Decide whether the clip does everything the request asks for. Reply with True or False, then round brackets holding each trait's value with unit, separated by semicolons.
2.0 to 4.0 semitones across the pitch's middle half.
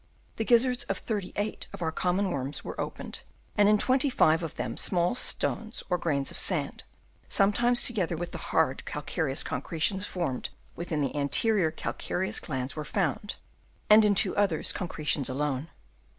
False (5.5 semitones)